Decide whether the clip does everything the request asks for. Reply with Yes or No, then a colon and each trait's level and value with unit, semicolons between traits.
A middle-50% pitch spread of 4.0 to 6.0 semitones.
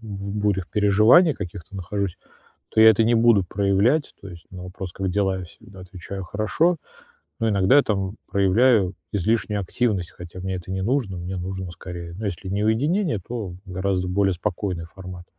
No: average, 2.9 semitones